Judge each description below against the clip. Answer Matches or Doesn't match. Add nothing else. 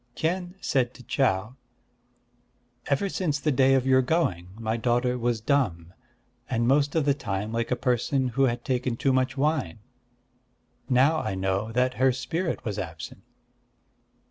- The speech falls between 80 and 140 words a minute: Doesn't match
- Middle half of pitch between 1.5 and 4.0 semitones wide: Matches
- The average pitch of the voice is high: Doesn't match